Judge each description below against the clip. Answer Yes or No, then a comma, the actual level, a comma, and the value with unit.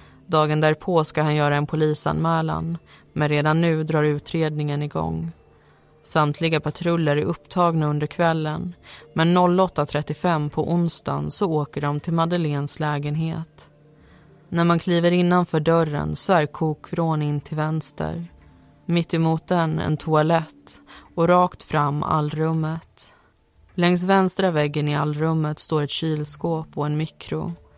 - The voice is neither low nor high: Yes, medium, 155 Hz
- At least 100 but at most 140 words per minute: Yes, slow, 125 wpm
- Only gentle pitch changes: Yes, narrow, 2.0 semitones